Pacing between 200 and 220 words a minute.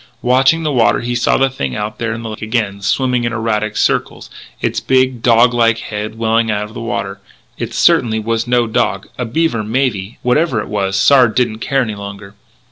Yes: fast, 205 wpm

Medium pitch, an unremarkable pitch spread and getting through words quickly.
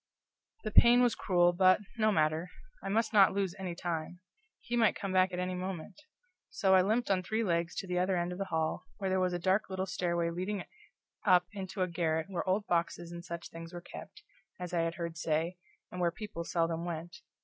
No: medium, 180 Hz; narrow, 2.3 semitones; fast, 215 wpm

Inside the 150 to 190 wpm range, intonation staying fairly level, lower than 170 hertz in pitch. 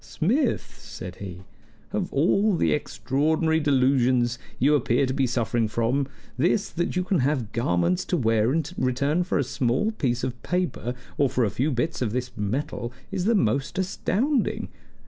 No: average, 165 wpm; wide, 5.5 semitones; low, 135 Hz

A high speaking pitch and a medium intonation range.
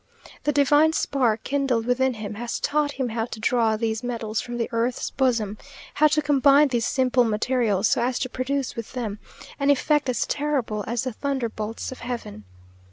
Yes: high, 245 Hz; average, 3.6 semitones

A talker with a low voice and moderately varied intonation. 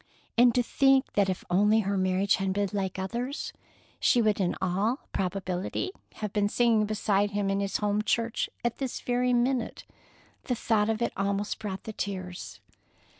No: high, 205 Hz; average, 3.2 semitones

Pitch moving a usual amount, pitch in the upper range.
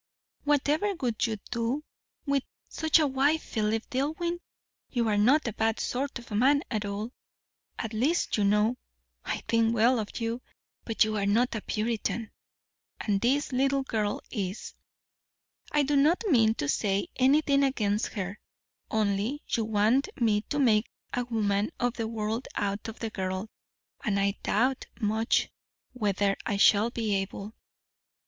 Yes: average, 4.1 semitones; high, 225 Hz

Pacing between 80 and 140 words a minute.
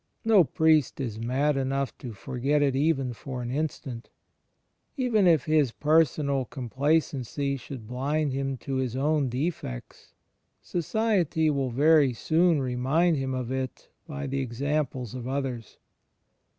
Yes: slow, 135 wpm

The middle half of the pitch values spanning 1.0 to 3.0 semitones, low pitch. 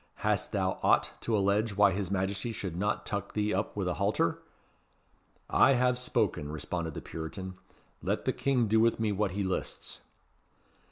Yes: average, 2.7 semitones; low, 100 Hz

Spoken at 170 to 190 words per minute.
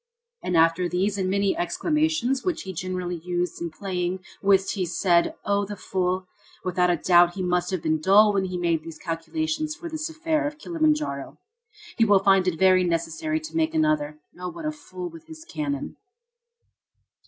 Yes: average, 185 wpm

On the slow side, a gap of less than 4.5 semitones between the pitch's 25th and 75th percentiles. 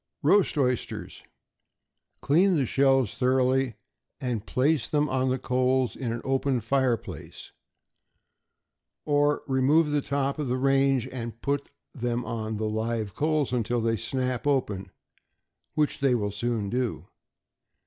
Yes: slow, 130 wpm; average, 3.0 semitones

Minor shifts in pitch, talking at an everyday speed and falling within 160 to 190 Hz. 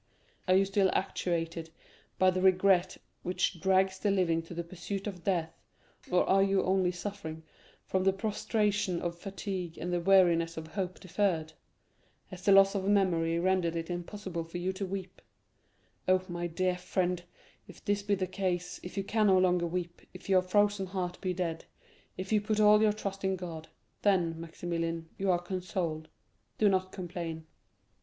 Yes: narrow, 2.2 semitones; average, 170 wpm; medium, 185 Hz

